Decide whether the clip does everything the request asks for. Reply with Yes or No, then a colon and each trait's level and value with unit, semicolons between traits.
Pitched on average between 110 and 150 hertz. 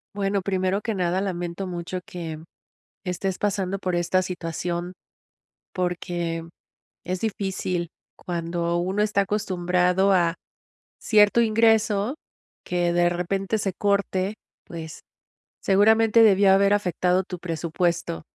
No: medium, 185 Hz